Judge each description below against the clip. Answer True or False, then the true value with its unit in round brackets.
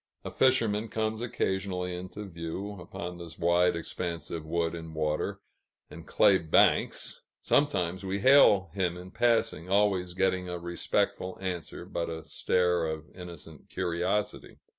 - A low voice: True (90 Hz)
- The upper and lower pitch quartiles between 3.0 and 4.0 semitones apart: False (2.5 semitones)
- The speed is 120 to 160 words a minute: True (140 wpm)